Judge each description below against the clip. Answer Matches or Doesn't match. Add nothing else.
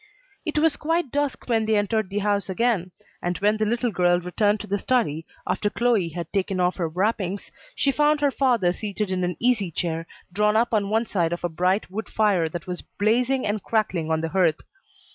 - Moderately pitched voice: Doesn't match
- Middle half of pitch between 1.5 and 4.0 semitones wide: Doesn't match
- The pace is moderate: Doesn't match